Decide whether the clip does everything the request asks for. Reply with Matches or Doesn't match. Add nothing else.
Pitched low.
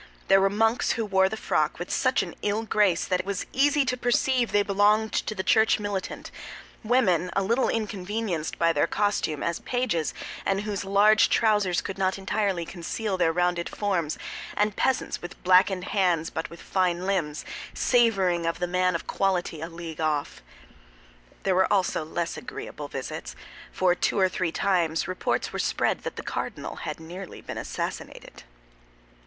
Doesn't match